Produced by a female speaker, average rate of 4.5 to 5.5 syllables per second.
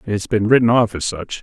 No: male; 5.4 syllables/s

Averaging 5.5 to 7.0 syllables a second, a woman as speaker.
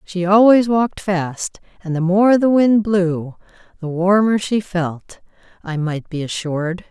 No: 4.0 syllables/s; female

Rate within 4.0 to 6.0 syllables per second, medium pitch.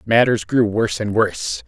No: 5.1 syllables/s; low, 110 Hz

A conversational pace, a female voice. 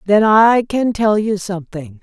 Yes: average, 180 wpm; female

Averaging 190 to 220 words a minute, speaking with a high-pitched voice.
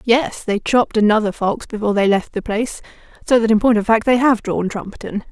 Yes: fast, 205 wpm; high, 220 Hz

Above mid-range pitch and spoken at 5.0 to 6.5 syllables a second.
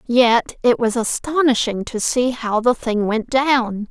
No: high, 240 Hz; 3.8 syllables/s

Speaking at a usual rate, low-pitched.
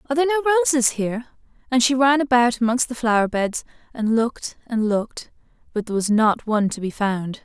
No: average, 195 wpm; high, 240 Hz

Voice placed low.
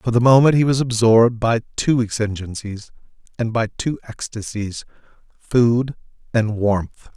Yes: low, 115 Hz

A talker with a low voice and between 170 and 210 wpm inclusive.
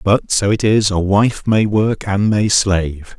Yes: low, 100 Hz; fast, 205 wpm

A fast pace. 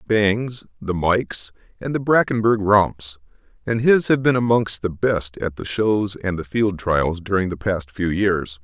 No: average, 180 wpm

